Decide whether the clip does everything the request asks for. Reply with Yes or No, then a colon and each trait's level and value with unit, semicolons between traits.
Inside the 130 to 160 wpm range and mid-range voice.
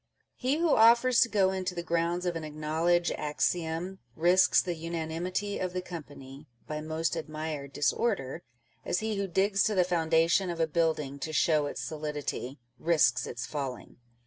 No: average, 170 wpm; medium, 165 Hz